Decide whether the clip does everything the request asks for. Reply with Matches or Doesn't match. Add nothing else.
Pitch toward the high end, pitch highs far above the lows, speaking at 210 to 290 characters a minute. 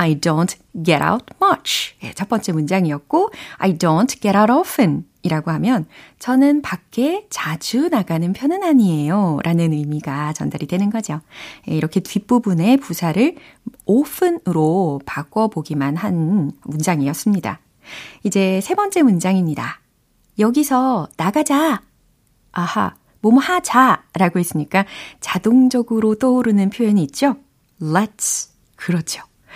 Doesn't match